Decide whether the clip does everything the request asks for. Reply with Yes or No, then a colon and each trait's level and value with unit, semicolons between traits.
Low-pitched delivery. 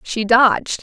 No: high, 230 Hz